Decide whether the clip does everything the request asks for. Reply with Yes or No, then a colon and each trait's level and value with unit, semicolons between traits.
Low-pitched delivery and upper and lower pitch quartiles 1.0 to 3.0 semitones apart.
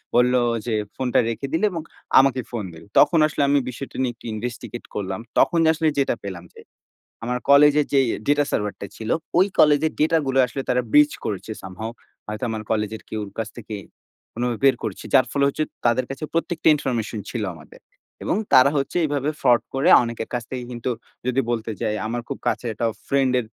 No: low, 125 Hz; average, 3.8 semitones